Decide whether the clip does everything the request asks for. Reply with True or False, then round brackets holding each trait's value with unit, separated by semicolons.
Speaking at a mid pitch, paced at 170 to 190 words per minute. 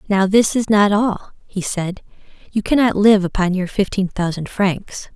False (200 Hz; 175 wpm)